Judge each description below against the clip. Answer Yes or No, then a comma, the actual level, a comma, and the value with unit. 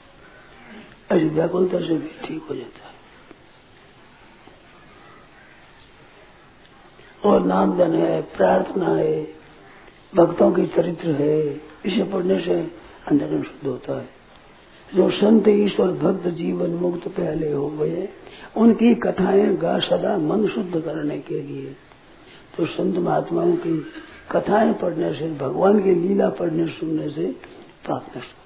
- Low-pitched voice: No, medium, 175 Hz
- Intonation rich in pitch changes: No, average, 3.6 semitones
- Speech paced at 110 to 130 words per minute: Yes, average, 120 wpm